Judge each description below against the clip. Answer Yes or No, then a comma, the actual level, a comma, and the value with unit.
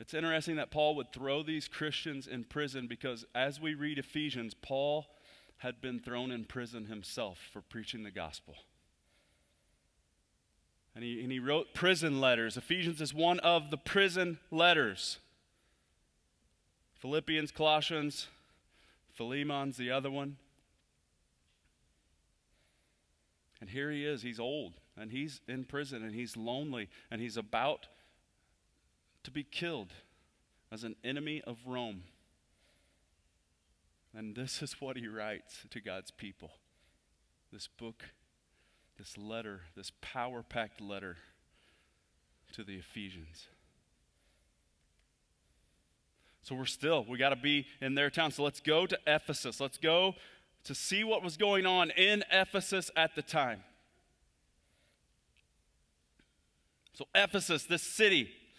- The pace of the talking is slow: Yes, slow, 125 wpm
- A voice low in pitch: Yes, low, 120 Hz